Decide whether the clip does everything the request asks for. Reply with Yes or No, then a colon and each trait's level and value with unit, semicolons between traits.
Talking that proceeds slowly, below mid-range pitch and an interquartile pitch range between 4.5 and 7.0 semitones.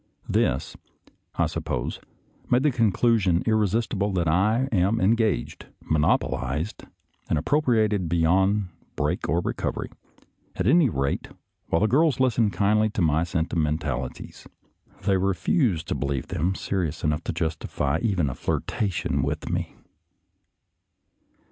Yes: slow, 125 wpm; very low, 95 Hz; wide, 5.4 semitones